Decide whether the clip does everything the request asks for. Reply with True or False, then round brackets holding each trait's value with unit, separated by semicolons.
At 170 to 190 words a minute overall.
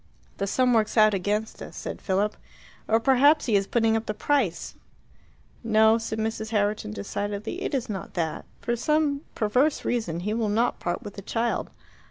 True (180 wpm)